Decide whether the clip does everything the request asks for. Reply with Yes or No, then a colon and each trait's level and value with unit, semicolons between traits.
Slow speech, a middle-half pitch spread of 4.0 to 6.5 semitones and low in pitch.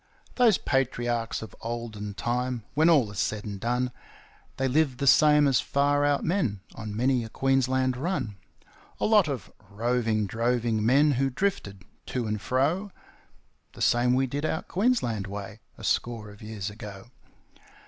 No: average, 160 wpm; average, 4.4 semitones; low, 125 Hz